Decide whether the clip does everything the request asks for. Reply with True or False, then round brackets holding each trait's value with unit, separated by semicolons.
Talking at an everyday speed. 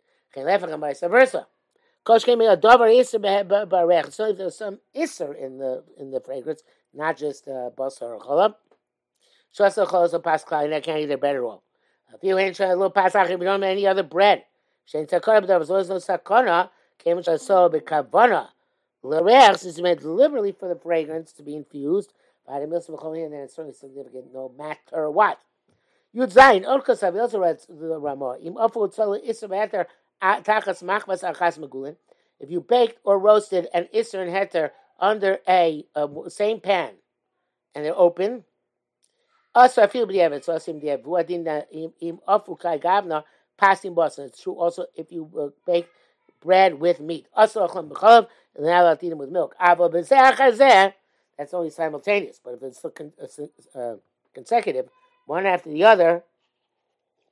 False (130 wpm)